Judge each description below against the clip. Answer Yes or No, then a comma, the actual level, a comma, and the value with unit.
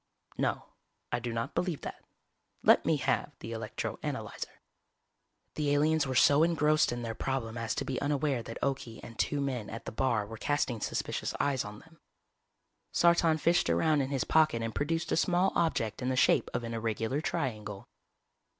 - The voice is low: Yes, low, 130 Hz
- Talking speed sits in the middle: Yes, average, 185 wpm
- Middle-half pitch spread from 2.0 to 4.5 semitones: No, average, 5.0 semitones